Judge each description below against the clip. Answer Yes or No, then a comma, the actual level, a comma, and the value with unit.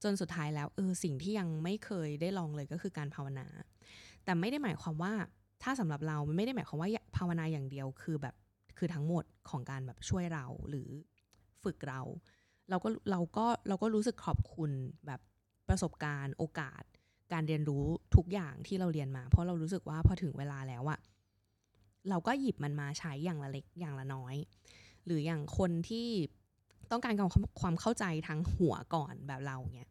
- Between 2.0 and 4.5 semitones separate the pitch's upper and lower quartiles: No, average, 5.2 semitones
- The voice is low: No, medium, 155 Hz